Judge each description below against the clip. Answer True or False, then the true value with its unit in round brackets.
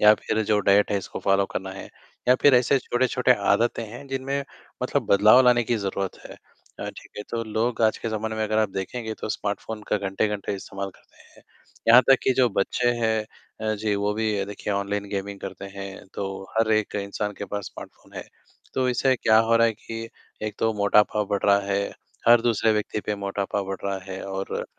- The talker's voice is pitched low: True (105 Hz)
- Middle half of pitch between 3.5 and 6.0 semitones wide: False (2.4 semitones)